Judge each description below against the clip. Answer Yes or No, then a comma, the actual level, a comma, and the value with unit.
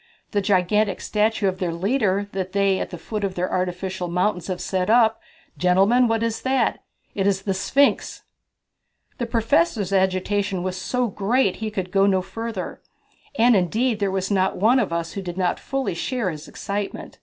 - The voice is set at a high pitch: Yes, high, 195 Hz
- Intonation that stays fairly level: No, average, 3.2 semitones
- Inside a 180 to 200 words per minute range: Yes, average, 185 wpm